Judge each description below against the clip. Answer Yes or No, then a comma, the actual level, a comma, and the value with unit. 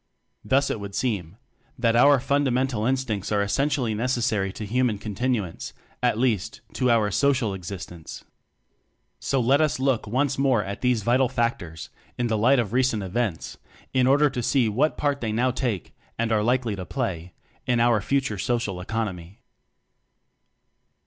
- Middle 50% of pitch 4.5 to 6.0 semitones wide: No, average, 4.0 semitones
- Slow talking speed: No, average, 155 wpm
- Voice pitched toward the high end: No, low, 120 Hz